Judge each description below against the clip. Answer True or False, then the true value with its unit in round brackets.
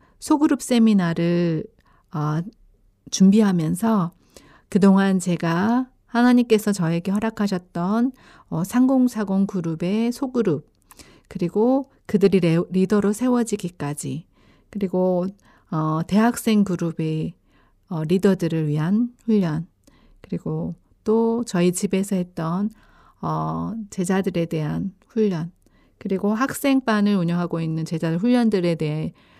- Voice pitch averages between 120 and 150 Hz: False (190 Hz)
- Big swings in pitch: False (4.7 semitones)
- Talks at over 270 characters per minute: False (245 characters per minute)